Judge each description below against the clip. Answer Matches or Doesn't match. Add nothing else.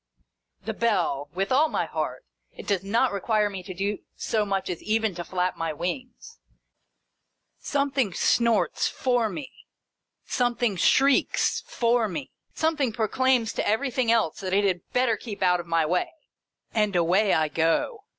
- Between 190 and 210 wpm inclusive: Doesn't match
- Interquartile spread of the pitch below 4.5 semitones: Doesn't match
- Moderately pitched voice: Doesn't match